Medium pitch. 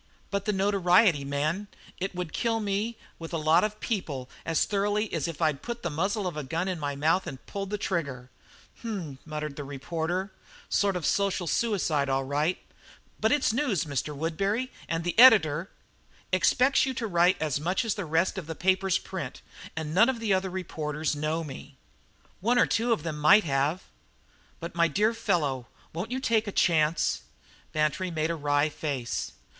Yes: medium, 175 Hz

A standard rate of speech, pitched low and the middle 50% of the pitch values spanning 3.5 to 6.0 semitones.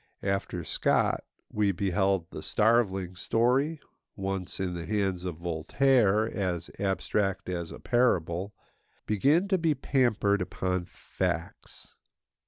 No: slow, 105 wpm; very low, 95 Hz; average, 3.9 semitones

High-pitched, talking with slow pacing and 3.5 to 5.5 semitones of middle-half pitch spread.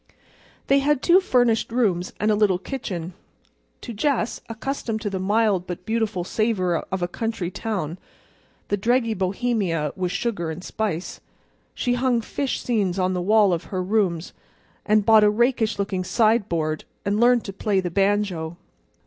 No: high, 205 Hz; average, 160 wpm; average, 3.9 semitones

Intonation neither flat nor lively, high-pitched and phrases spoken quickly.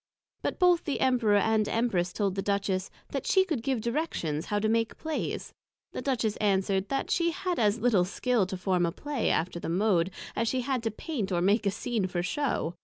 Yes: average, 5.0 semitones; high, 215 Hz; fast, 215 wpm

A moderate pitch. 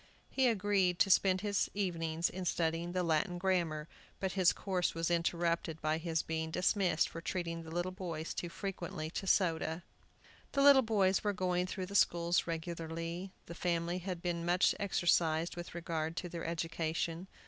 Yes: medium, 175 Hz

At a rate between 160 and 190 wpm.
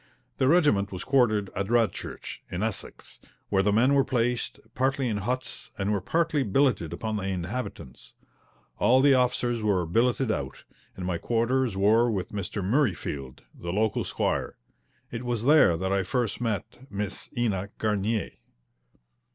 No: average, 150 wpm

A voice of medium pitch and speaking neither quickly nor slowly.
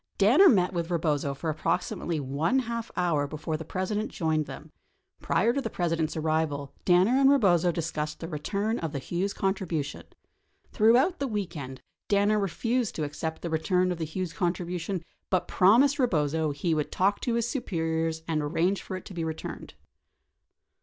Yes: medium, 175 Hz; average, 170 wpm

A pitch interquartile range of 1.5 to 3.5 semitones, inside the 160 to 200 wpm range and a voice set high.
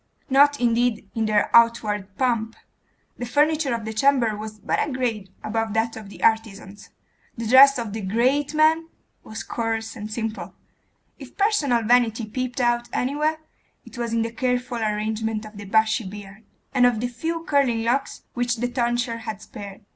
Yes: narrow, 2.6 semitones; average, 170 wpm; high, 230 Hz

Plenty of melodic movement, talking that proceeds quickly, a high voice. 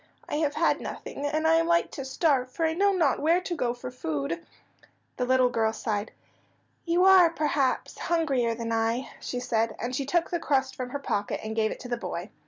Yes: wide, 5.8 semitones; fast, 215 wpm; very high, 260 Hz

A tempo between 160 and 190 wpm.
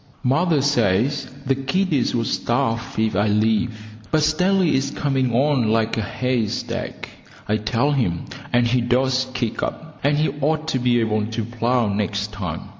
Yes: average, 165 wpm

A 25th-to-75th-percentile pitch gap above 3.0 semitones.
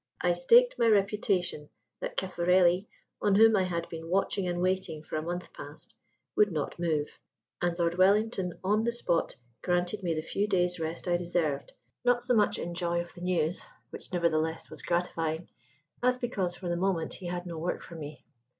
No: narrow, 2.6 semitones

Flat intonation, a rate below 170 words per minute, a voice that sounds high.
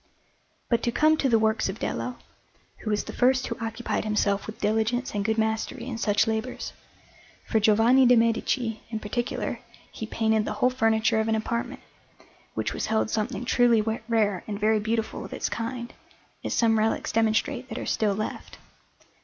No: narrow, 1.7 semitones; average, 180 wpm; high, 225 Hz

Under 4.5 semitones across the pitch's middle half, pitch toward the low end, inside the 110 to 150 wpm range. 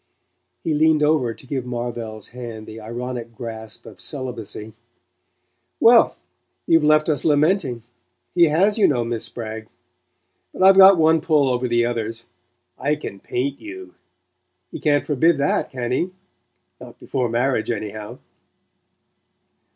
No: average, 4.9 semitones; low, 125 Hz; slow, 135 wpm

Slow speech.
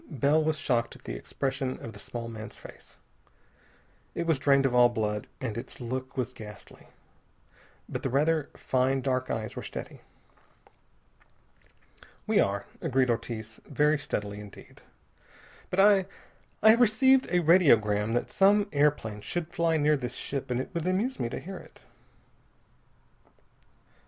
No: average, 150 wpm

